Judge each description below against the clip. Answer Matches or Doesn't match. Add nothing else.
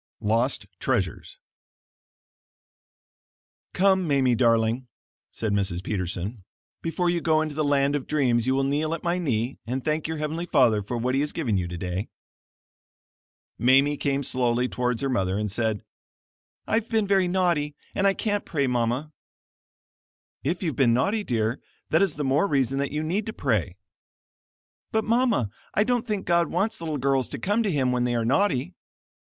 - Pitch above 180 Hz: Doesn't match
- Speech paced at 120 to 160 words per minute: Doesn't match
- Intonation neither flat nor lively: Doesn't match